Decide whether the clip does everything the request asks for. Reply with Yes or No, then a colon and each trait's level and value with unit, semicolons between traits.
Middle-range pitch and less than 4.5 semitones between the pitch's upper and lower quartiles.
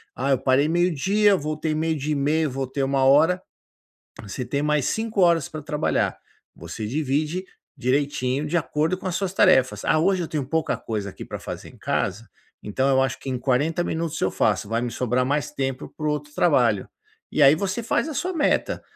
Yes: medium, 150 Hz; average, 3.9 semitones